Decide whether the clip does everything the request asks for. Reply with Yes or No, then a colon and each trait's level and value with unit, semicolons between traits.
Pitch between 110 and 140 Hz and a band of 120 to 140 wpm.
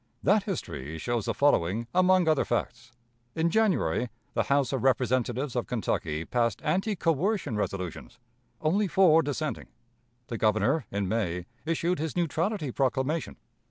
Yes: low, 135 Hz; slow, 135 wpm